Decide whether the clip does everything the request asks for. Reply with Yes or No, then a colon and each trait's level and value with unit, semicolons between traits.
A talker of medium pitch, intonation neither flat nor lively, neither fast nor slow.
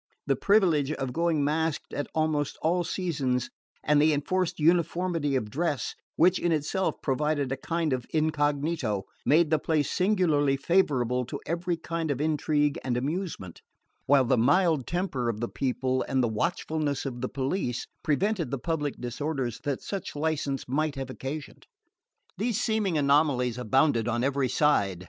Yes: medium, 145 Hz; average, 4.0 semitones; average, 155 wpm